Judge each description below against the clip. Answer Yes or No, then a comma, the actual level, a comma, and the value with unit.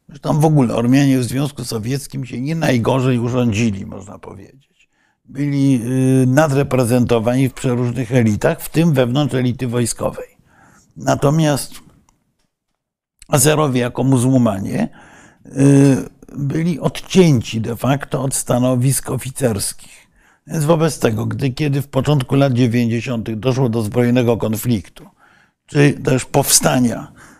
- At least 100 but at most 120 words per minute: Yes, slow, 110 wpm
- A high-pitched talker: No, low, 130 Hz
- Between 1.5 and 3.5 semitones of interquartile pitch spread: Yes, average, 2.8 semitones